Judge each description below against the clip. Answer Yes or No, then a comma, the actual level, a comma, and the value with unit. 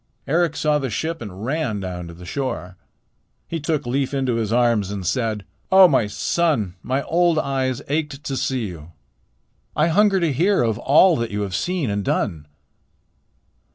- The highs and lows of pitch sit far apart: Yes, wide, 7.4 semitones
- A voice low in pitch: Yes, low, 130 Hz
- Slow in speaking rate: No, average, 175 wpm